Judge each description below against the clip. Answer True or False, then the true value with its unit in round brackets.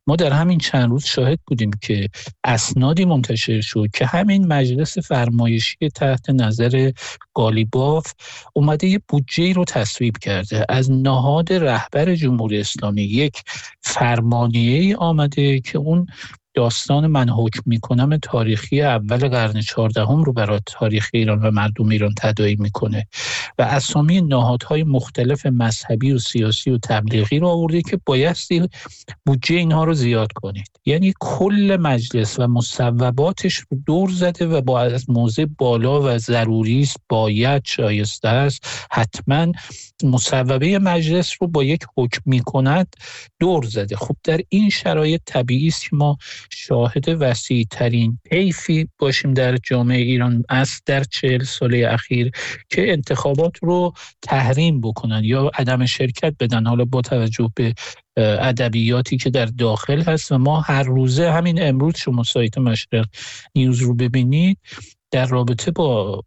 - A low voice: True (130 Hz)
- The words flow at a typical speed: True (140 wpm)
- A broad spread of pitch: False (4.6 semitones)